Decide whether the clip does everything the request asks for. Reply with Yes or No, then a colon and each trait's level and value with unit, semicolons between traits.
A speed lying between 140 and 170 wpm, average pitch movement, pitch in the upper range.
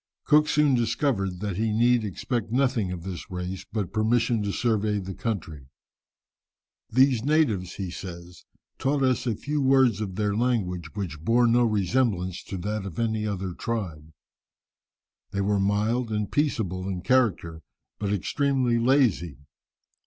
No: average, 145 wpm; average, 4.7 semitones; low, 105 Hz